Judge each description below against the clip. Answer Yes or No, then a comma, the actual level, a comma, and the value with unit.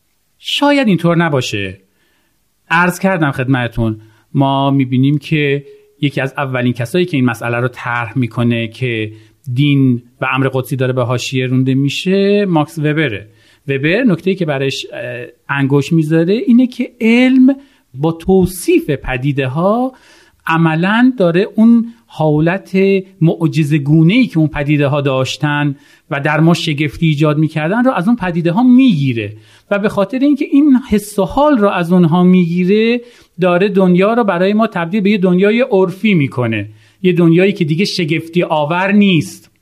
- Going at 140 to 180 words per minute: Yes, average, 150 wpm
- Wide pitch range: Yes, wide, 6.5 semitones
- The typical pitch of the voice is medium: Yes, medium, 165 Hz